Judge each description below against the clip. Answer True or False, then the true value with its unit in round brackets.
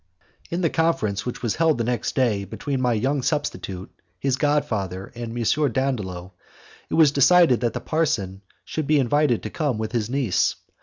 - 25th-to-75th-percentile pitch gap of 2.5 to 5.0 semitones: False (5.4 semitones)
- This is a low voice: True (125 Hz)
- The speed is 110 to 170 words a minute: False (185 wpm)